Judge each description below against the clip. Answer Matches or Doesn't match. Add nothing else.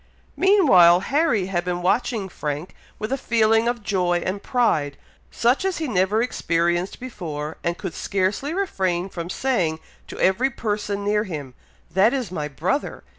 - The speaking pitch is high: Matches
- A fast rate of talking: Doesn't match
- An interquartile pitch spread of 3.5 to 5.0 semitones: Doesn't match